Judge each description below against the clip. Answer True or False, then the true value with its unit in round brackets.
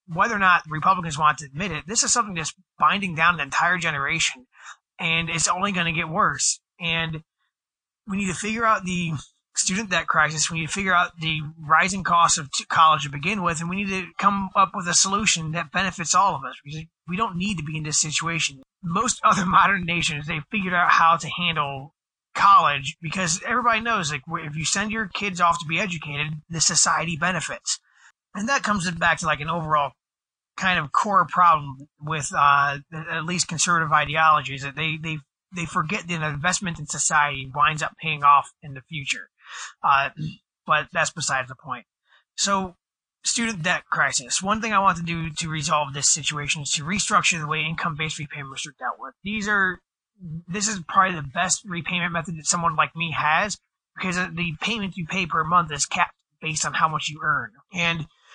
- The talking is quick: False (195 wpm)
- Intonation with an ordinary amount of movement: True (3.3 semitones)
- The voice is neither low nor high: True (165 Hz)